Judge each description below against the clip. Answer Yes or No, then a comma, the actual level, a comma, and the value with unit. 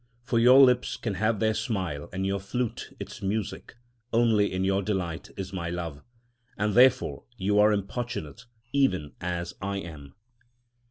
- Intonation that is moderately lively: Yes, average, 4.4 semitones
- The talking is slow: No, average, 155 wpm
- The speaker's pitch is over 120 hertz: No, low, 100 Hz